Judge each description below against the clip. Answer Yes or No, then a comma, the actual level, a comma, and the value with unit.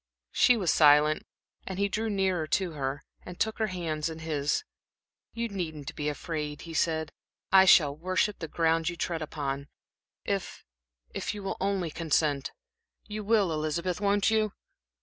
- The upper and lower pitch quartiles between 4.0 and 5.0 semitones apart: Yes, average, 4.3 semitones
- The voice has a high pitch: No, medium, 165 Hz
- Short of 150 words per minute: No, average, 160 wpm